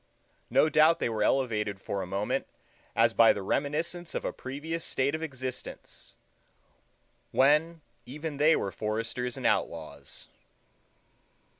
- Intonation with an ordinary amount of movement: No, wide, 6.3 semitones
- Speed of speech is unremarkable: No, slow, 130 wpm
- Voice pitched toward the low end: Yes, low, 130 Hz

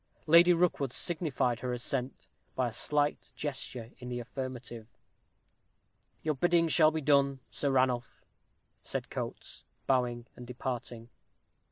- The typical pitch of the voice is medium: No, low, 130 Hz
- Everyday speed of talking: No, slow, 125 wpm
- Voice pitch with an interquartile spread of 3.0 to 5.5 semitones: Yes, average, 3.5 semitones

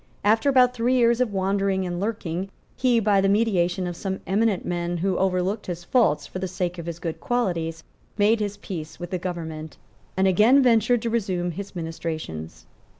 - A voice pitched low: No, high, 190 Hz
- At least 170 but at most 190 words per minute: Yes, average, 185 wpm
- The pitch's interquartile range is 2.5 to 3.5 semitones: No, average, 4.2 semitones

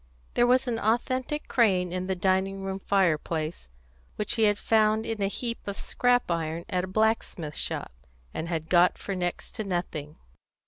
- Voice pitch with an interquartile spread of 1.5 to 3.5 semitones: No, average, 4.1 semitones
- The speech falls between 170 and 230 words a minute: Yes, average, 175 wpm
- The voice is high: Yes, high, 195 Hz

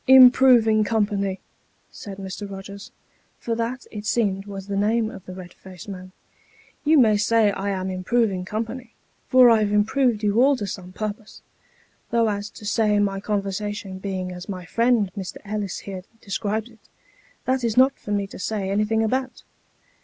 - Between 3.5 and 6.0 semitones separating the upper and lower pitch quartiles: No, average, 2.7 semitones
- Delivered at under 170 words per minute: No, average, 175 wpm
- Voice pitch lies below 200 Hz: No, high, 210 Hz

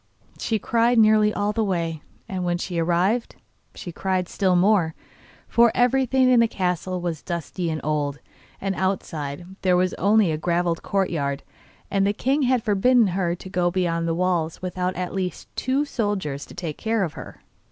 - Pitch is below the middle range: No, medium, 185 Hz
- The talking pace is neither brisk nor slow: Yes, average, 175 wpm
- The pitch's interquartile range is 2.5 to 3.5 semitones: No, average, 3.9 semitones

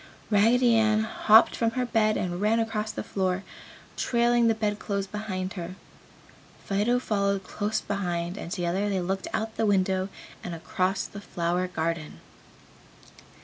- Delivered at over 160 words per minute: No, average, 145 wpm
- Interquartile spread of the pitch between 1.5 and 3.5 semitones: Yes, average, 3.0 semitones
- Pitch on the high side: Yes, high, 200 Hz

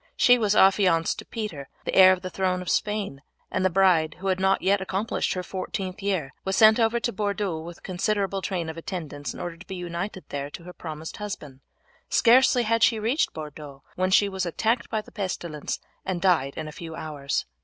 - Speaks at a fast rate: Yes, fast, 210 wpm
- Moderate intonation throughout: Yes, average, 3.7 semitones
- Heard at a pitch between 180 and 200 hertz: Yes, medium, 185 Hz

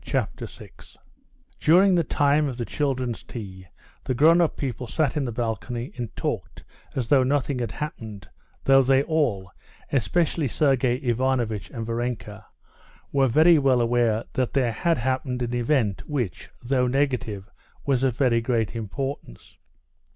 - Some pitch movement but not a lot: Yes, average, 3.3 semitones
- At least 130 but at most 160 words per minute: Yes, average, 150 wpm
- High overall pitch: No, low, 125 Hz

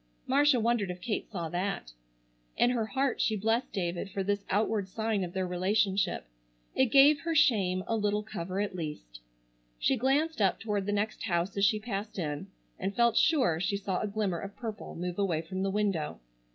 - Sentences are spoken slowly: No, average, 190 wpm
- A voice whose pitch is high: Yes, high, 200 Hz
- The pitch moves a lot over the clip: No, average, 3.4 semitones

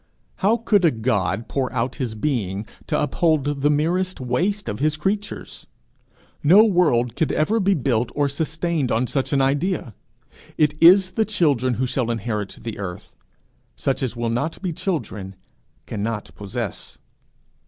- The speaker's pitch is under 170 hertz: Yes, medium, 140 Hz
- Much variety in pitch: Yes, wide, 6.6 semitones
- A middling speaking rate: Yes, average, 155 wpm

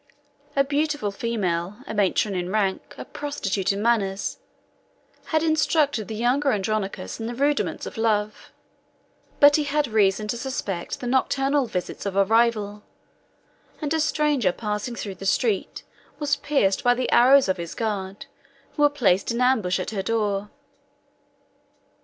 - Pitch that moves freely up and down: Yes, wide, 5.7 semitones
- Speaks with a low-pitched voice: No, high, 225 Hz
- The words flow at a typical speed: Yes, average, 150 wpm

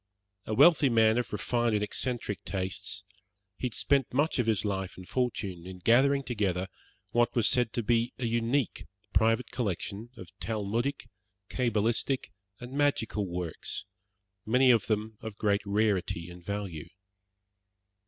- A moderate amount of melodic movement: Yes, average, 3.5 semitones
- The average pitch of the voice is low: Yes, low, 110 Hz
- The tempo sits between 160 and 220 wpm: No, average, 145 wpm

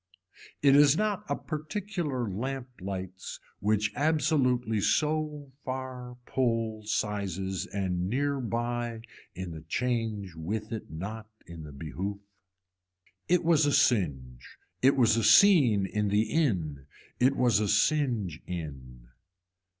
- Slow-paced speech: Yes, slow, 125 wpm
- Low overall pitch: Yes, low, 110 Hz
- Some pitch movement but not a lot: No, wide, 6.3 semitones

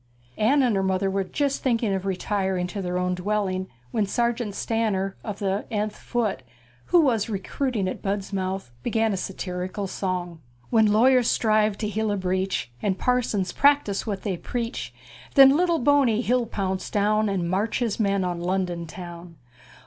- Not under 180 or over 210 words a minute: Yes, average, 185 wpm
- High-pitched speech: Yes, high, 200 Hz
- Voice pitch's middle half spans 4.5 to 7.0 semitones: No, average, 3.4 semitones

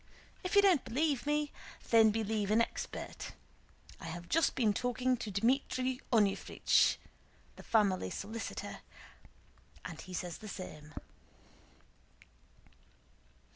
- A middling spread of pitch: Yes, average, 4.5 semitones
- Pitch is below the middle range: No, high, 225 Hz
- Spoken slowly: Yes, slow, 110 wpm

